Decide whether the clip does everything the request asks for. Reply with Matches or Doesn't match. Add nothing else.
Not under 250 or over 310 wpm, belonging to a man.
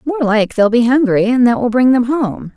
Doesn't match